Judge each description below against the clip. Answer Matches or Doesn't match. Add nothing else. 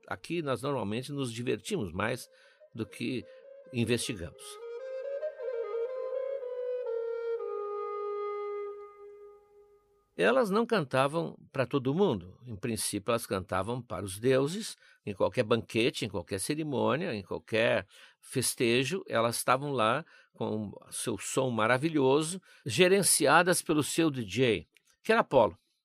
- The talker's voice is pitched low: Doesn't match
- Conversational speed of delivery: Doesn't match